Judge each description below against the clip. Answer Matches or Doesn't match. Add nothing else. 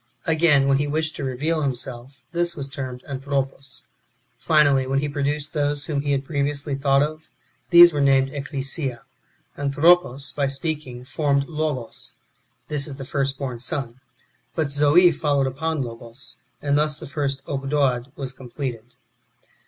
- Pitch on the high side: Doesn't match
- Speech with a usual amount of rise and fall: Doesn't match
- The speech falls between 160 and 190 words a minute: Doesn't match